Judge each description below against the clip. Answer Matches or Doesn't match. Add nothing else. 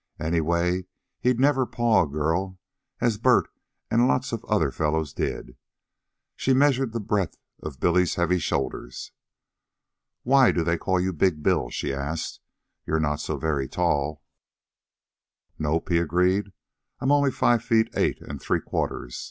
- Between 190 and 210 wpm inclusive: Doesn't match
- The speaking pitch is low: Matches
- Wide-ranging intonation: Matches